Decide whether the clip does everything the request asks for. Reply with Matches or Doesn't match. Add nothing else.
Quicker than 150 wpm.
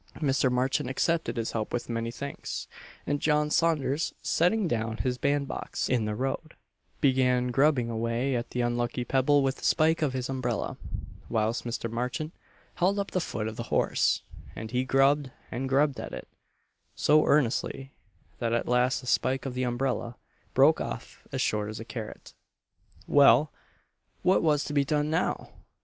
Matches